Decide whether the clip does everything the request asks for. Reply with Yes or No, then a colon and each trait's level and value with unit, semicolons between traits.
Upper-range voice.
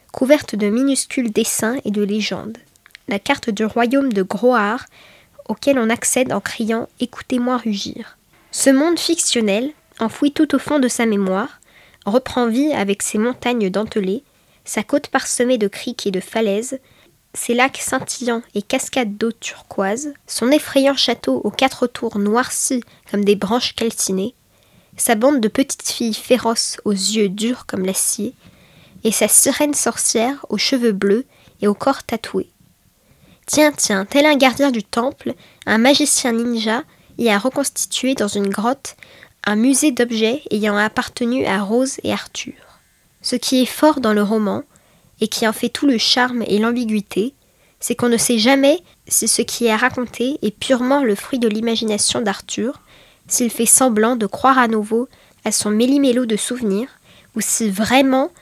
Yes: high, 235 Hz